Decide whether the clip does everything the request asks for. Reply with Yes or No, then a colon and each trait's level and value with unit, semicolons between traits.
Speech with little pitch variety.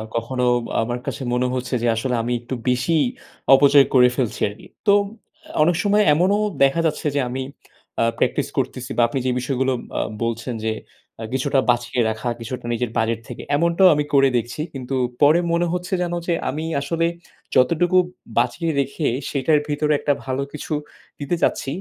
No: average, 4.1 semitones